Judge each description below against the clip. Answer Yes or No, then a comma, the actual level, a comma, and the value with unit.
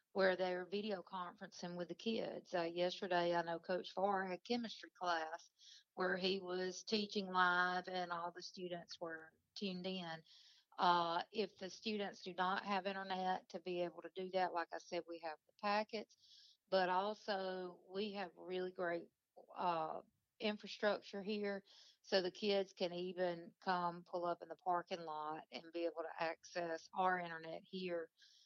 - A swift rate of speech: No, average, 165 wpm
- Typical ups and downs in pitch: No, narrow, 2.1 semitones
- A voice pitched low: No, medium, 185 Hz